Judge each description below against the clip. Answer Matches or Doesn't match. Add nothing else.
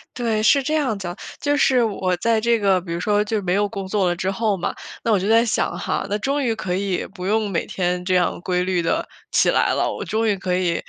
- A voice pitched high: Matches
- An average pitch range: Matches